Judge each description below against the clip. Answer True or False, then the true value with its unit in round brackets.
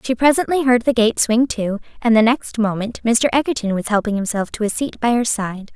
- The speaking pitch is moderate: False (230 Hz)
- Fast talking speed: True (230 wpm)